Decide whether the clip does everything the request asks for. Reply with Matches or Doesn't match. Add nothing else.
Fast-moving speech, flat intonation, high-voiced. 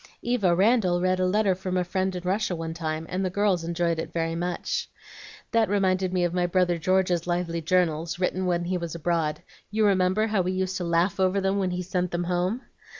Doesn't match